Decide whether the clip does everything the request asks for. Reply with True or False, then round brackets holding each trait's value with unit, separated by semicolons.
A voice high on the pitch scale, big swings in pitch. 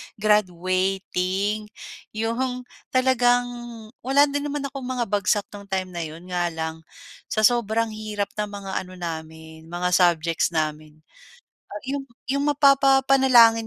True (205 Hz; 5.8 semitones)